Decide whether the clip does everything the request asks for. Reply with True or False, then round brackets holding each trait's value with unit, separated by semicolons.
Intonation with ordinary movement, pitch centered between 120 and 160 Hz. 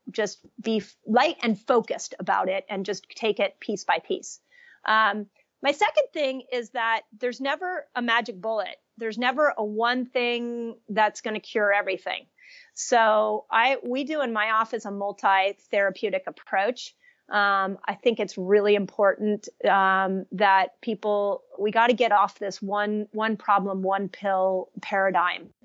False (3.6 semitones; 215 Hz)